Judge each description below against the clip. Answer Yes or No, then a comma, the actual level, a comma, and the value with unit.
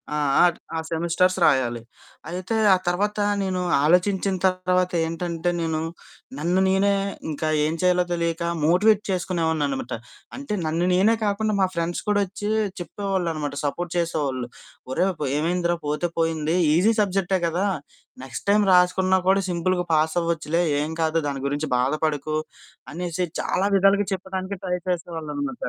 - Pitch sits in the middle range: Yes, medium, 175 Hz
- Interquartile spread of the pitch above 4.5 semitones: No, average, 2.8 semitones